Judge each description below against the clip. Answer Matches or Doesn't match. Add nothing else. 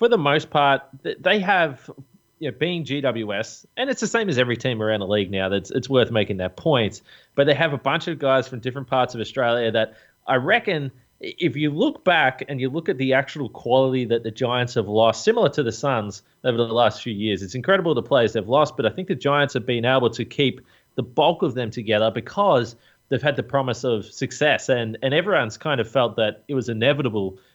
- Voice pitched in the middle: Doesn't match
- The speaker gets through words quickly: Matches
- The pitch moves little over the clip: Doesn't match